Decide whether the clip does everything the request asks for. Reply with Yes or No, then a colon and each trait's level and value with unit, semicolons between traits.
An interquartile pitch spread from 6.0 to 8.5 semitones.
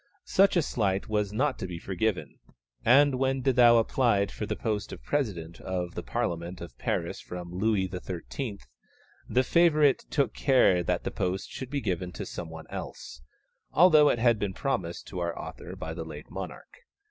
Yes: wide, 6.7 semitones